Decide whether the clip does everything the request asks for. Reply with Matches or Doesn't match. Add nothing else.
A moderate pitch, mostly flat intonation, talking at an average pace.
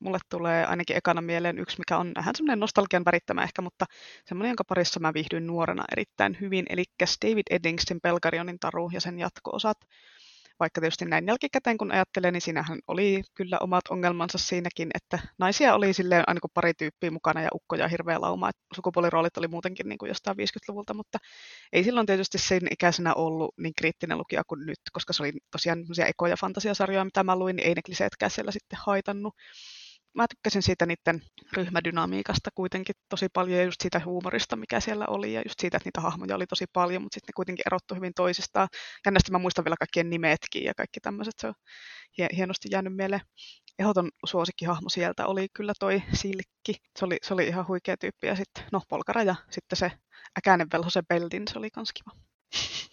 Doesn't match